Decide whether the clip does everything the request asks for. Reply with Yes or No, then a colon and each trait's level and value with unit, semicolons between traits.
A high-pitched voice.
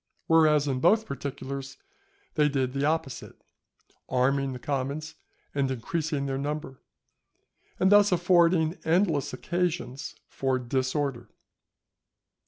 No: medium, 140 Hz